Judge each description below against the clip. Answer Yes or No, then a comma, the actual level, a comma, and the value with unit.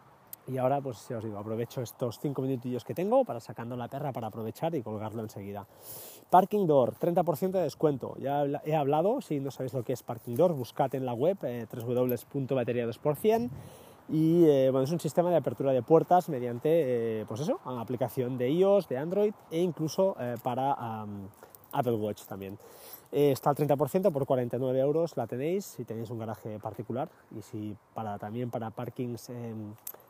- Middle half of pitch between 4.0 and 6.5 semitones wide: Yes, average, 4.8 semitones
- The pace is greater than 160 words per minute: Yes, average, 185 wpm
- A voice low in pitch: Yes, low, 130 Hz